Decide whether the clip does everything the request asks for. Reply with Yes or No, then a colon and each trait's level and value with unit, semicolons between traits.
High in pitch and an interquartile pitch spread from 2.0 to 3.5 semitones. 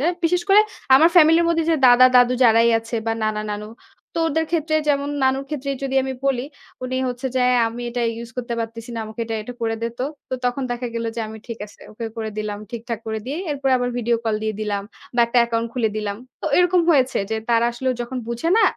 Yes: high, 245 Hz; average, 3.2 semitones